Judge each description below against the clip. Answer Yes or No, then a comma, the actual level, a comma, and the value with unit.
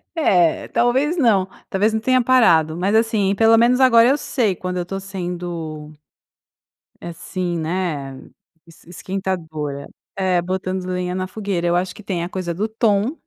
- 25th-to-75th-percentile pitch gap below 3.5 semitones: No, average, 4.2 semitones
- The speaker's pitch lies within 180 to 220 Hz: Yes, medium, 185 Hz